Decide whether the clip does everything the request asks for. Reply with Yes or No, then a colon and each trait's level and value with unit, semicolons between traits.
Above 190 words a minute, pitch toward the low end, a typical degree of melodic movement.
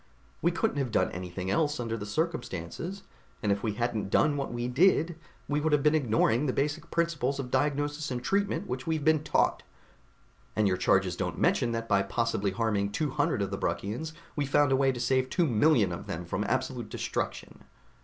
No: average, 200 wpm; low, 130 Hz; wide, 5.9 semitones